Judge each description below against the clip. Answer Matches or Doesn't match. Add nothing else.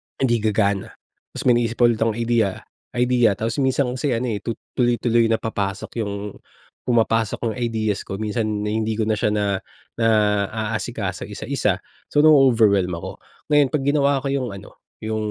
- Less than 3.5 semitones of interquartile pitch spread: Matches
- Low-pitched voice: Matches